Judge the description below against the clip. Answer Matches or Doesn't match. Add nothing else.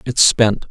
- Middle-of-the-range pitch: Doesn't match